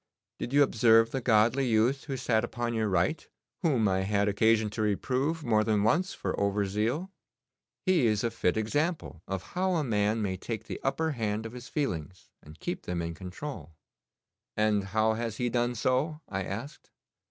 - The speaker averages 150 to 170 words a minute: No, average, 185 wpm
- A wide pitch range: No, average, 4.6 semitones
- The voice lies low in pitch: Yes, low, 110 Hz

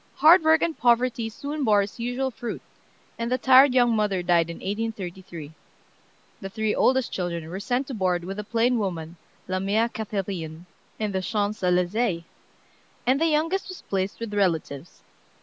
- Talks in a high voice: Yes, high, 210 Hz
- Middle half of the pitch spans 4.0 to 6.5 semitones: Yes, average, 5.1 semitones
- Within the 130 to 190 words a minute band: Yes, average, 165 wpm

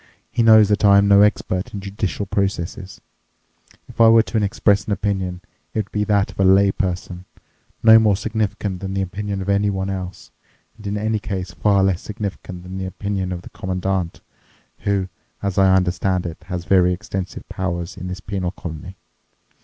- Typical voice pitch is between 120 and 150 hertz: No, very low, 95 Hz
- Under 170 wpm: No, average, 185 wpm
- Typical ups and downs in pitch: No, narrow, 1.9 semitones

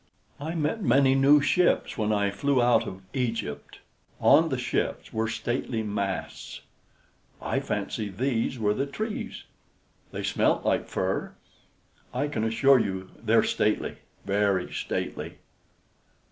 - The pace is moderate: No, slow, 130 wpm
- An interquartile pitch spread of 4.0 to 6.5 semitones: Yes, average, 5.2 semitones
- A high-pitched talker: No, low, 120 Hz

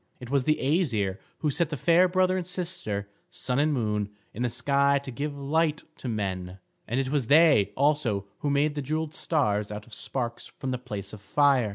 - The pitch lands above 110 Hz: Yes, medium, 140 Hz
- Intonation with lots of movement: Yes, wide, 5.8 semitones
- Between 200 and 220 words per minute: Yes, fast, 205 wpm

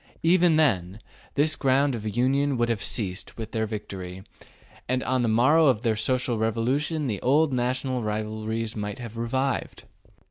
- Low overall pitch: Yes, low, 120 Hz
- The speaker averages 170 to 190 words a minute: No, average, 155 wpm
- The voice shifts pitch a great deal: No, average, 3.7 semitones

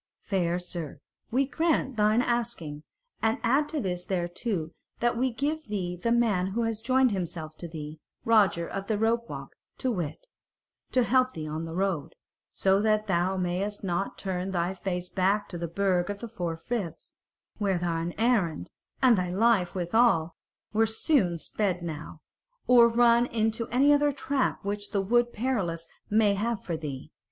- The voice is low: No, high, 200 Hz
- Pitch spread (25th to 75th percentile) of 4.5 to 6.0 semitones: Yes, average, 5.1 semitones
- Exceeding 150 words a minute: Yes, average, 165 wpm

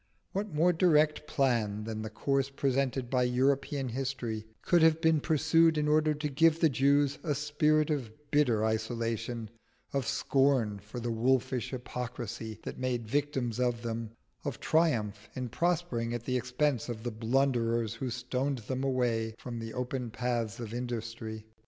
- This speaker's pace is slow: No, average, 160 wpm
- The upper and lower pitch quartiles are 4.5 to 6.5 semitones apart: No, average, 3.9 semitones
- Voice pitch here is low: Yes, low, 125 Hz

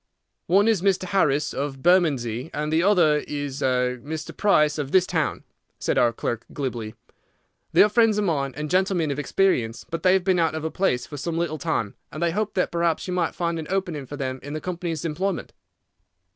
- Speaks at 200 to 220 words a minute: Yes, fast, 205 wpm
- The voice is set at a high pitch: No, medium, 160 Hz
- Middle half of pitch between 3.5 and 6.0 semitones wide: Yes, average, 4.4 semitones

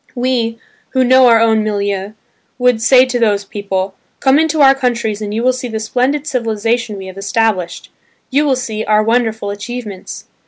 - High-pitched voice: Yes, high, 225 Hz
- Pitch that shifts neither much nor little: Yes, average, 3.3 semitones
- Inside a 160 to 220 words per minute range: Yes, average, 180 wpm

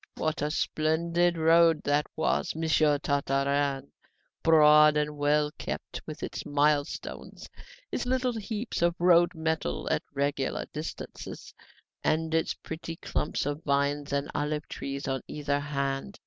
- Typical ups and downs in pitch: No, narrow, 2.3 semitones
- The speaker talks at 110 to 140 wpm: Yes, slow, 135 wpm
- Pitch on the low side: No, medium, 150 Hz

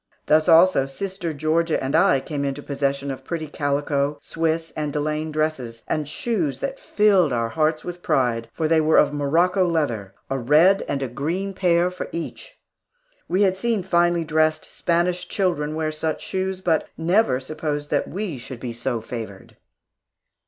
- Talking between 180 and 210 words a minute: No, average, 165 wpm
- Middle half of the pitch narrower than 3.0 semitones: No, average, 4.0 semitones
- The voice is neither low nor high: Yes, medium, 155 Hz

